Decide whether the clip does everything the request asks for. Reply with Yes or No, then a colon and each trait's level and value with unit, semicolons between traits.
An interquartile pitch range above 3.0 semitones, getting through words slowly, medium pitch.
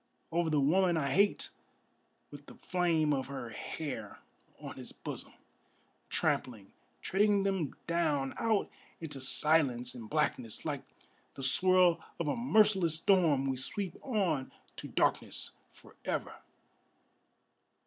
Yes: wide, 5.4 semitones; slow, 120 wpm; medium, 160 Hz